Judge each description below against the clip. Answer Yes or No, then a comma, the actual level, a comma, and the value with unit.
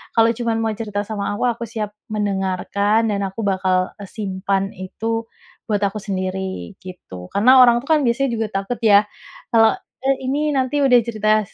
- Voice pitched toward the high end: Yes, high, 215 Hz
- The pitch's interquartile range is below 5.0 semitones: Yes, average, 3.1 semitones